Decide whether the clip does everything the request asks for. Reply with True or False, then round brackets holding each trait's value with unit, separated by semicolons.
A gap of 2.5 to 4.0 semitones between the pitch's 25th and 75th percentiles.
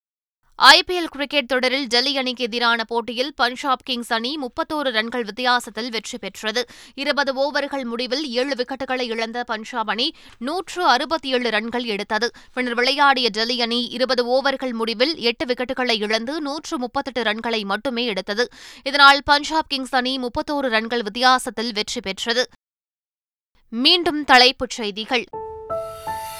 True (2.9 semitones)